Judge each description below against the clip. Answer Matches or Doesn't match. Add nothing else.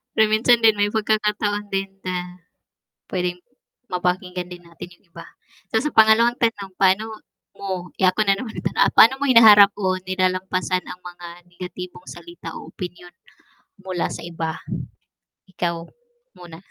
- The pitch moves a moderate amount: Matches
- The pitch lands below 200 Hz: Matches